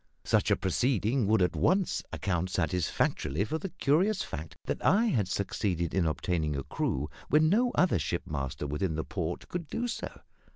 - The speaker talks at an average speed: Yes, average, 170 wpm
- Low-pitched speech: Yes, very low, 95 Hz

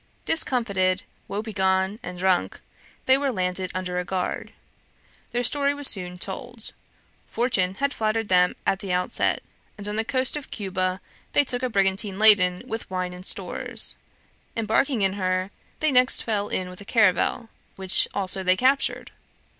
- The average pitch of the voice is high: Yes, high, 200 Hz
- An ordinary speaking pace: Yes, average, 155 wpm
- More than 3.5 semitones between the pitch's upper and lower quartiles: Yes, average, 4.3 semitones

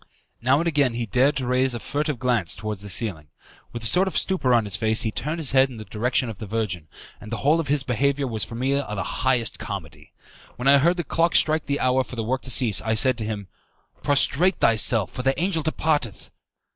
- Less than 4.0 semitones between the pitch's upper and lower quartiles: No, average, 4.3 semitones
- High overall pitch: No, low, 125 Hz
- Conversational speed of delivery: No, fast, 235 wpm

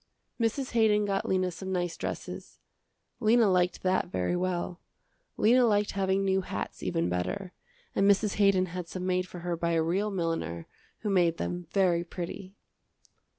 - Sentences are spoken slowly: No, average, 160 wpm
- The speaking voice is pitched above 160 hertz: Yes, medium, 185 Hz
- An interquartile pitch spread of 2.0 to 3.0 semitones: Yes, narrow, 2.5 semitones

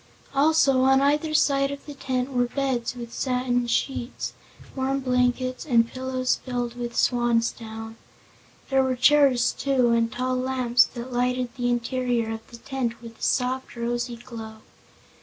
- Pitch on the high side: Yes, very high, 250 Hz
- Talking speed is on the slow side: No, average, 150 wpm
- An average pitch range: No, narrow, 1.8 semitones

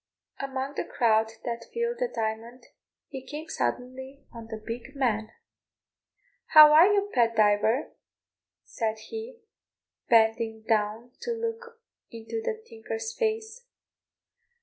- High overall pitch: Yes, very high, 250 Hz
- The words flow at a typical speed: No, slow, 120 wpm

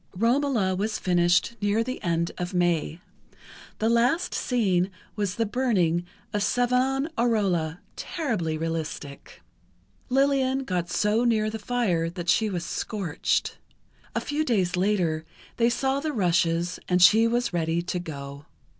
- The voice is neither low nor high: No, high, 200 Hz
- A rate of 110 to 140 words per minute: Yes, slow, 135 wpm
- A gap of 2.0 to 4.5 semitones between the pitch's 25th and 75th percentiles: No, wide, 5.6 semitones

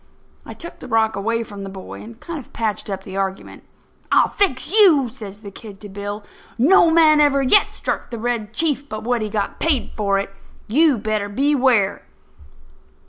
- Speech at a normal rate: Yes, average, 190 wpm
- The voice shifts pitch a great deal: Yes, wide, 5.7 semitones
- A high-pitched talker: Yes, high, 225 Hz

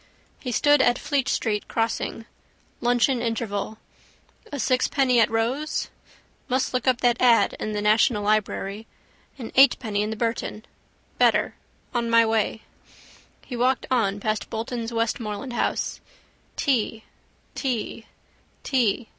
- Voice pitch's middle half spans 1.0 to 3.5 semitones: Yes, narrow, 2.6 semitones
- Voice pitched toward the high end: Yes, high, 230 Hz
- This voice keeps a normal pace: No, slow, 125 wpm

